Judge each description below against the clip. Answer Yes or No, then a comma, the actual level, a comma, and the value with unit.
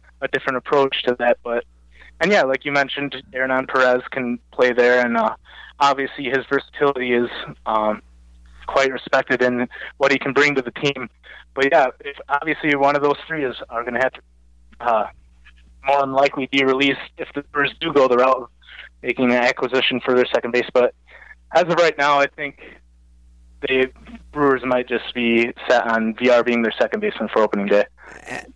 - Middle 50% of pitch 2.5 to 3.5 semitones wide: Yes, average, 2.9 semitones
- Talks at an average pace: Yes, average, 190 wpm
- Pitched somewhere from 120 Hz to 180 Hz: Yes, low, 130 Hz